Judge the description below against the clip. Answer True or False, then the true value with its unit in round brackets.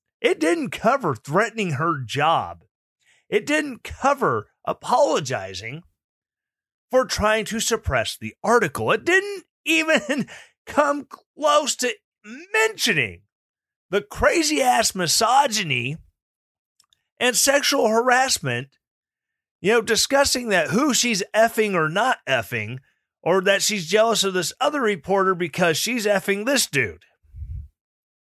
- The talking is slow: True (110 wpm)